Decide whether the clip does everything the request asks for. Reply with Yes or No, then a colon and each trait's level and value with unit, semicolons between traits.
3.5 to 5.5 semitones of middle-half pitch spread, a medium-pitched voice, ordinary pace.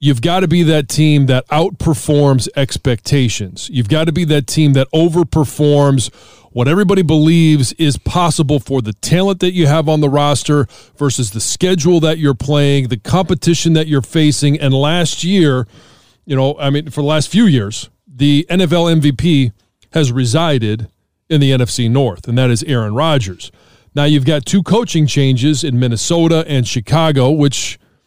Yes: average, 3.9 semitones; medium, 145 Hz; average, 170 wpm